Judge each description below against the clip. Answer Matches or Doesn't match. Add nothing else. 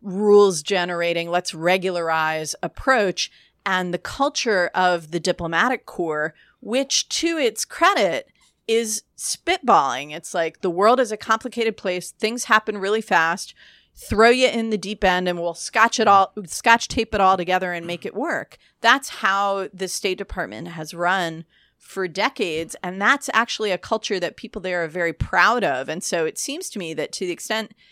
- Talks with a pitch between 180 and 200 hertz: Matches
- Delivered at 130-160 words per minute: Doesn't match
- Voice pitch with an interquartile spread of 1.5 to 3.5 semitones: Doesn't match